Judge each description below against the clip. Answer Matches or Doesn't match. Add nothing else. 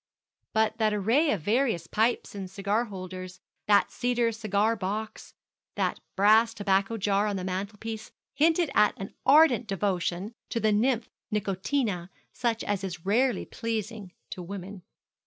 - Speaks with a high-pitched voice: Matches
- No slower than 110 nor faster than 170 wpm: Matches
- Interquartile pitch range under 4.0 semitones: Matches